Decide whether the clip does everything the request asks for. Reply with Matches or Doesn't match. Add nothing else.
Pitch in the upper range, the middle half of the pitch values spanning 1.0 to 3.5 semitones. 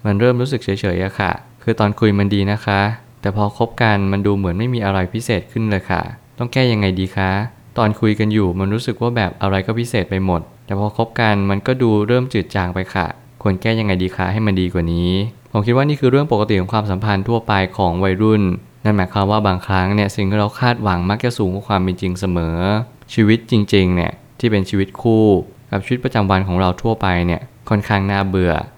Doesn't match